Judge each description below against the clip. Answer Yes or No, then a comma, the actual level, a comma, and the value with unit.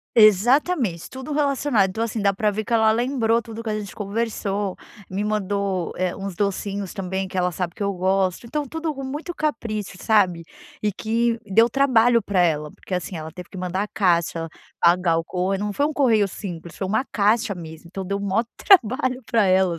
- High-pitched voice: Yes, high, 205 Hz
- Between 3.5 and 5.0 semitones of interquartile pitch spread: Yes, average, 3.9 semitones